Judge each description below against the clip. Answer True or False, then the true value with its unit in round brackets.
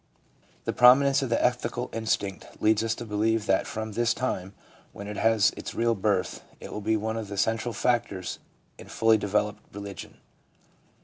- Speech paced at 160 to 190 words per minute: True (175 wpm)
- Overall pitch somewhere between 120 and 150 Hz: False (110 Hz)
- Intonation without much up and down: True (2.2 semitones)